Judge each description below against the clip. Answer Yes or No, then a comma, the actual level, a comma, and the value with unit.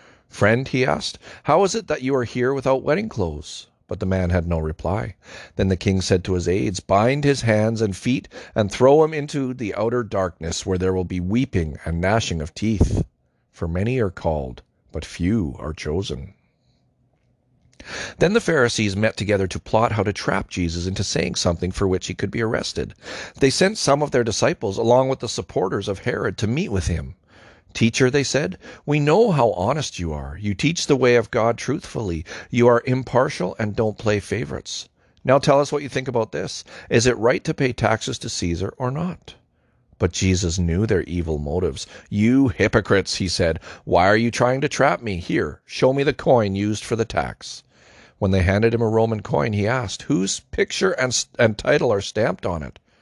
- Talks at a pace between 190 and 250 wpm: Yes, average, 200 wpm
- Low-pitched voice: Yes, low, 110 Hz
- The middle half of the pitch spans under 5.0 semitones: No, wide, 5.6 semitones